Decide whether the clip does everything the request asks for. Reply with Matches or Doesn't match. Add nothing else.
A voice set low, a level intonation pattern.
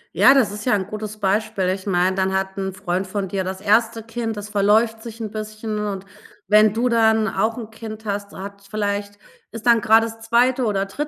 Doesn't match